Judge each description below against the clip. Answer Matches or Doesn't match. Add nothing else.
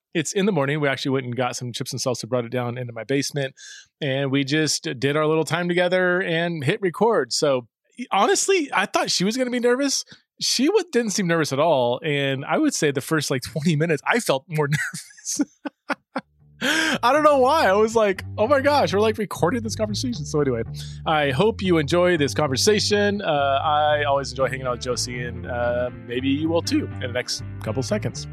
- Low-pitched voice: Doesn't match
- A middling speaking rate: Doesn't match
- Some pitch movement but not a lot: Doesn't match